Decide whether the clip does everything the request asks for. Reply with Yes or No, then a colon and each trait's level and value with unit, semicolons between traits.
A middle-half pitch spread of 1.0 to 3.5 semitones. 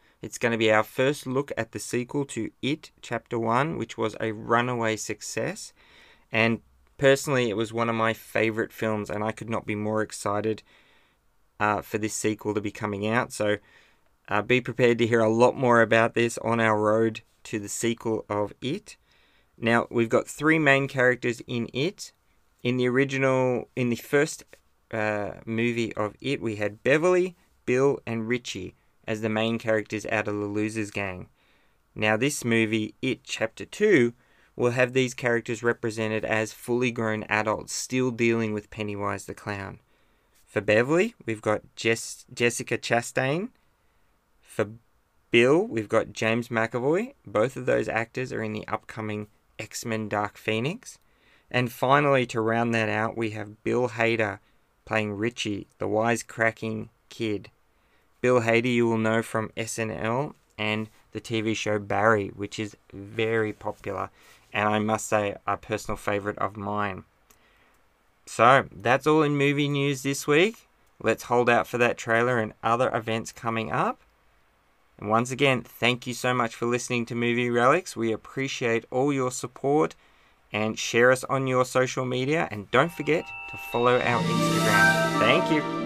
Yes: narrow, 2.5 semitones